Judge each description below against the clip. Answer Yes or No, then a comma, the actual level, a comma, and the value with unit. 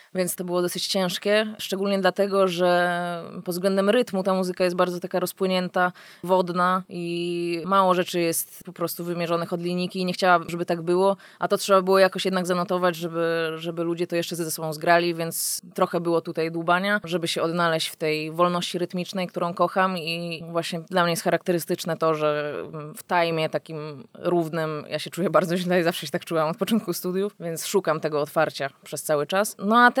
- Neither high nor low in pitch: Yes, medium, 175 Hz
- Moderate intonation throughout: No, narrow, 1.9 semitones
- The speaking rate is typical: No, fast, 190 wpm